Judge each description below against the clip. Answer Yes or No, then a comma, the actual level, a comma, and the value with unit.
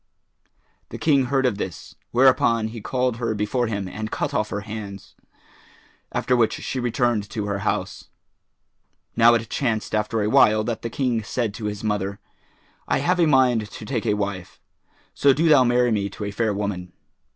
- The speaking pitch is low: Yes, low, 110 Hz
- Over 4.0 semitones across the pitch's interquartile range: No, average, 3.2 semitones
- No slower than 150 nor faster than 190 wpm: Yes, average, 185 wpm